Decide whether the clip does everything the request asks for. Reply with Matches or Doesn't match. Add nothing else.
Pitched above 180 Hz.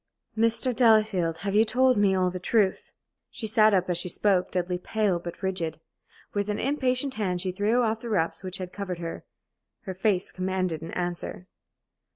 Matches